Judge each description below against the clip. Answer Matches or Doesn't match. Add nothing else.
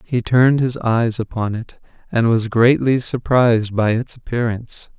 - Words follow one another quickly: Doesn't match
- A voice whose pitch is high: Doesn't match